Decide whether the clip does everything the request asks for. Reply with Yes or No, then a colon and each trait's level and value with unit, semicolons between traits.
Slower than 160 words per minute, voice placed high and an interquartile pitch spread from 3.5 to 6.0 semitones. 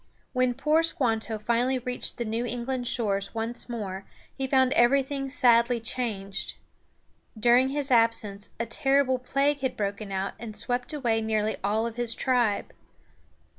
No: average, 140 wpm; high, 240 Hz; average, 3.0 semitones